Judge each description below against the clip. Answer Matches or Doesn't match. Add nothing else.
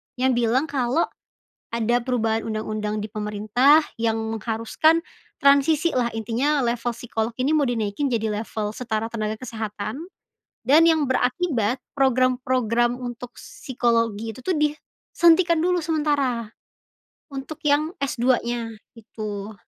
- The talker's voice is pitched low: Doesn't match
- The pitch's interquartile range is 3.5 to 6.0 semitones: Matches